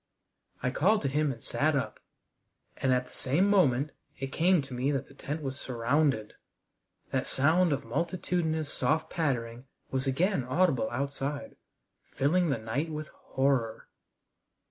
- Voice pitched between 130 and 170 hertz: Yes, medium, 140 Hz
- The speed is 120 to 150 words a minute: Yes, average, 145 wpm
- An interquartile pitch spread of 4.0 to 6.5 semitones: No, average, 3.6 semitones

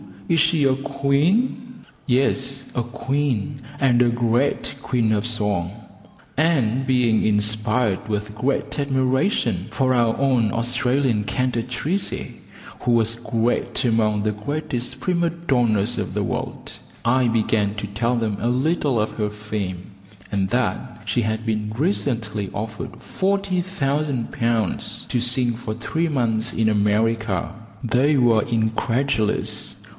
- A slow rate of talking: Yes, slow, 130 wpm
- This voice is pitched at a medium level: No, low, 120 Hz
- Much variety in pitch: No, average, 3.9 semitones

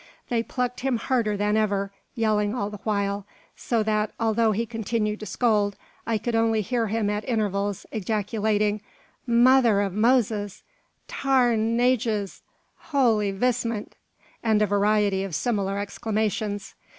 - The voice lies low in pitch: No, high, 215 Hz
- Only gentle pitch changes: Yes, narrow, 2.2 semitones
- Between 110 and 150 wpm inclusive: Yes, average, 140 wpm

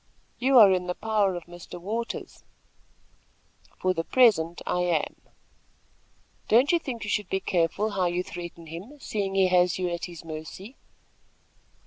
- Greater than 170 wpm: No, average, 155 wpm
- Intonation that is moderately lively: Yes, average, 3.7 semitones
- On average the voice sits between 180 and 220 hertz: Yes, medium, 185 Hz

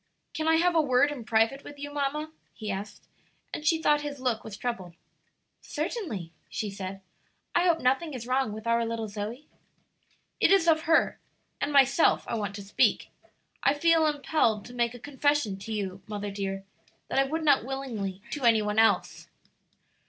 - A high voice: Yes, very high, 250 Hz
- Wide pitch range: Yes, wide, 5.8 semitones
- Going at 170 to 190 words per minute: Yes, average, 180 wpm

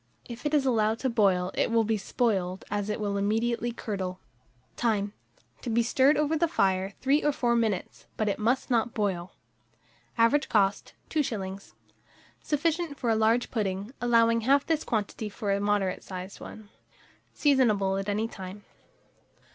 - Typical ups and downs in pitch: Yes, average, 3.5 semitones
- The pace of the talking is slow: No, average, 160 wpm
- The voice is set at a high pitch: Yes, high, 220 Hz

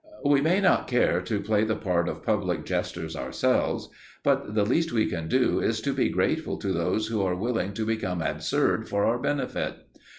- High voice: No, low, 105 Hz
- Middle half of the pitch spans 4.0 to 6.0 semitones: Yes, average, 4.8 semitones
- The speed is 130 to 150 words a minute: No, average, 195 wpm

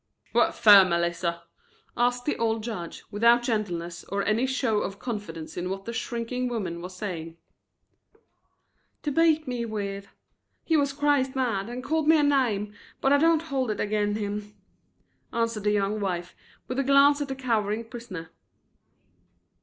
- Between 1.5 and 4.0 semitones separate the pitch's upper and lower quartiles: No, average, 4.7 semitones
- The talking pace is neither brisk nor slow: Yes, average, 160 wpm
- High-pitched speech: Yes, high, 225 Hz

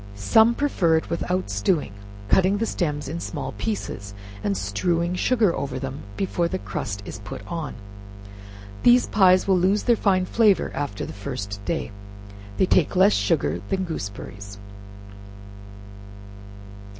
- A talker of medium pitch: Yes, medium, 165 Hz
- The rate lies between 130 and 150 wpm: Yes, average, 140 wpm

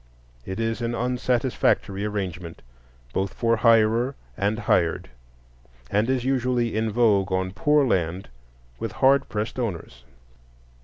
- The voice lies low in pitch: Yes, low, 110 Hz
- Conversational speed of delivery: No, slow, 120 wpm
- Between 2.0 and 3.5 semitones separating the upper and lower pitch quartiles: No, average, 4.0 semitones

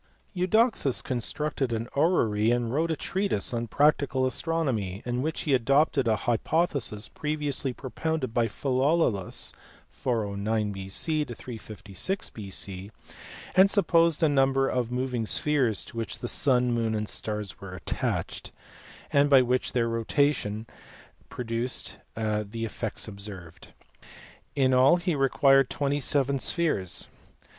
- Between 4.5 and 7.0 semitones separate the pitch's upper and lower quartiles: Yes, average, 4.8 semitones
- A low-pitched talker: Yes, low, 125 Hz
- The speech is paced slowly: Yes, slow, 125 wpm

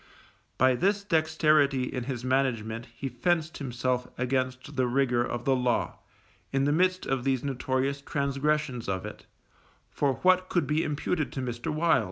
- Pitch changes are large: No, average, 3.4 semitones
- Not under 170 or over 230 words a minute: No, average, 160 wpm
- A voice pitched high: No, low, 135 Hz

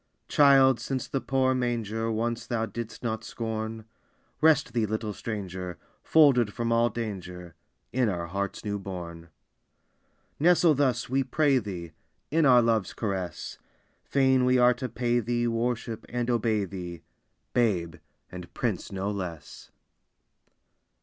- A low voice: Yes, low, 115 Hz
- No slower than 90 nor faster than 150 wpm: Yes, slow, 135 wpm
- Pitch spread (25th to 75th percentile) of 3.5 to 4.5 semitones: Yes, average, 4.1 semitones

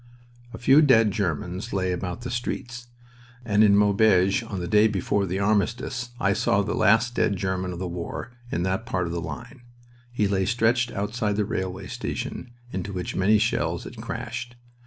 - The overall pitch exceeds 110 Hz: No, low, 105 Hz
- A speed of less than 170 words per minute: No, average, 180 wpm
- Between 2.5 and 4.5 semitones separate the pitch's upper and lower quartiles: Yes, average, 3.8 semitones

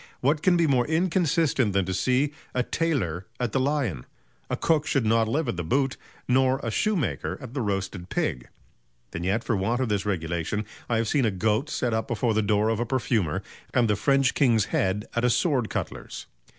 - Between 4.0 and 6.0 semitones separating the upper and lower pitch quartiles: Yes, average, 4.9 semitones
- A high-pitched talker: No, low, 115 Hz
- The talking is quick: Yes, fast, 210 wpm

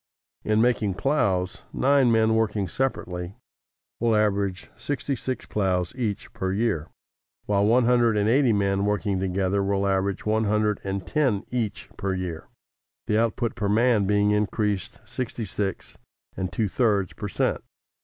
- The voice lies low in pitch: Yes, low, 105 Hz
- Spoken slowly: No, average, 150 wpm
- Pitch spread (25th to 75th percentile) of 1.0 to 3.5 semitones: Yes, average, 2.8 semitones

